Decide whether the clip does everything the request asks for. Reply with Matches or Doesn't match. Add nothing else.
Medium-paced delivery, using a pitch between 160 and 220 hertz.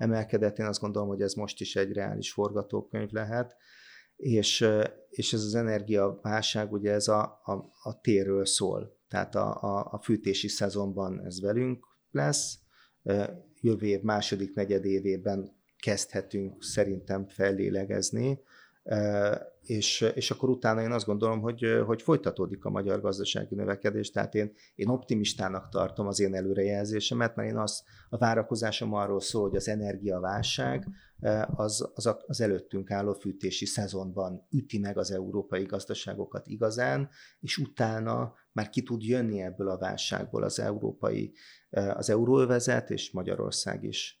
Doesn't match